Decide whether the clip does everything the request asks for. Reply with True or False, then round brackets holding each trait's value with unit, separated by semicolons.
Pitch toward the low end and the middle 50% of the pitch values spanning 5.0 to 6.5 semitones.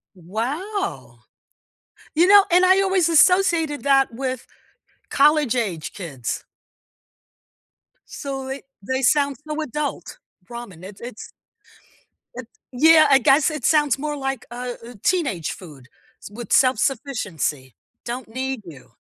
False (270 Hz; 5.4 semitones)